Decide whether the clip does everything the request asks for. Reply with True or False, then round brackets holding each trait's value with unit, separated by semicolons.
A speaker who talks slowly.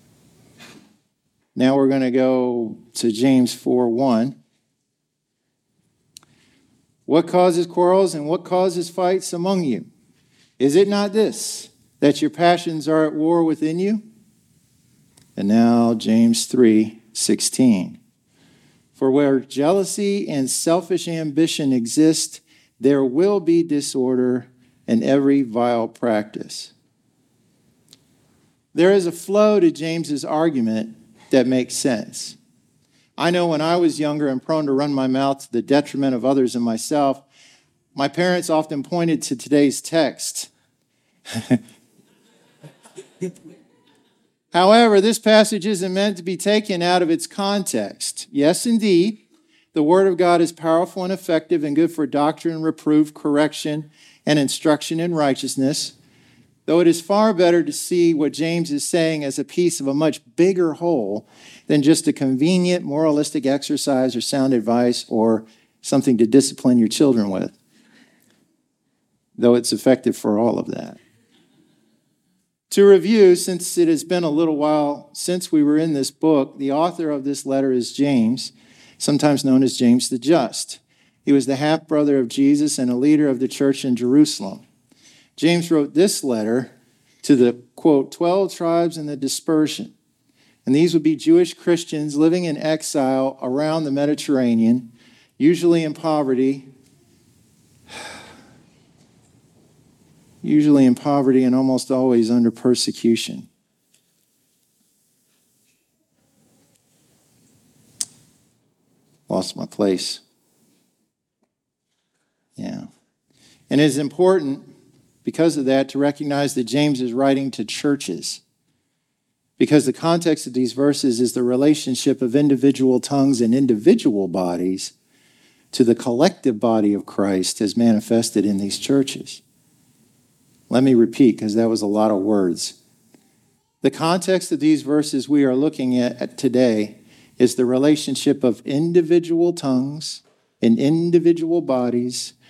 True (130 wpm)